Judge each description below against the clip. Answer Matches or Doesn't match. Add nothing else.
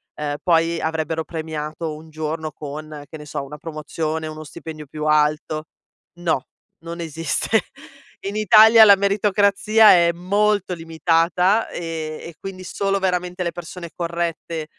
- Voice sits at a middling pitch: Matches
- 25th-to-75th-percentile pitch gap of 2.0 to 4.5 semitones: Matches